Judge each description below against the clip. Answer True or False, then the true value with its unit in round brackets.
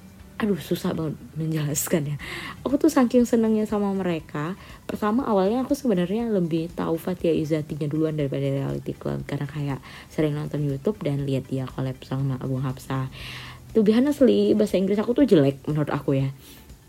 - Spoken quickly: True (165 wpm)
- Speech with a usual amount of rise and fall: False (7.2 semitones)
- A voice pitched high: False (160 Hz)